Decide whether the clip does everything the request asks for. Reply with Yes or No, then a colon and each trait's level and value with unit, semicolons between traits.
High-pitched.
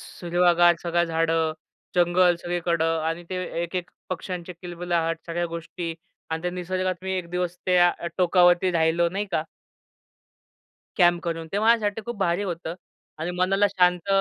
No: medium, 175 Hz